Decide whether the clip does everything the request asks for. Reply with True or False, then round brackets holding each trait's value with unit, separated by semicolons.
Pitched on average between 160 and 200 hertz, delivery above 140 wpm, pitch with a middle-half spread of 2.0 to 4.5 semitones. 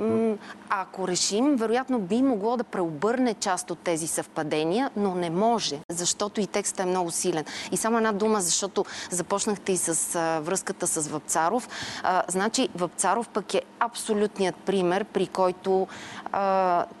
True (190 Hz; 150 wpm; 3.7 semitones)